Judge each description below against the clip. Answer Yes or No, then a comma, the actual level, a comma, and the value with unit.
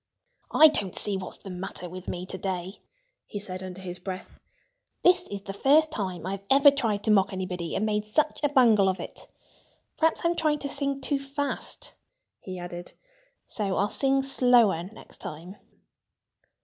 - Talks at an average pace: Yes, average, 175 wpm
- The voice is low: No, high, 205 Hz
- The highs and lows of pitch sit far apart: Yes, wide, 6.7 semitones